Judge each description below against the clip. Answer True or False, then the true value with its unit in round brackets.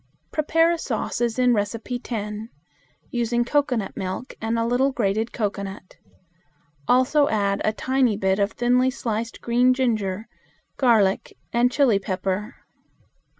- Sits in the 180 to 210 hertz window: False (230 Hz)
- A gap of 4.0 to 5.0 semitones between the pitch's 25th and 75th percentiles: False (3.5 semitones)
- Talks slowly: True (130 wpm)